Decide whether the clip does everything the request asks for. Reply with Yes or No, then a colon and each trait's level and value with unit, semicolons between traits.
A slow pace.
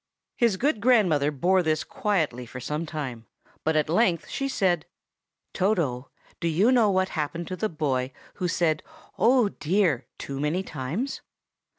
No: average, 155 wpm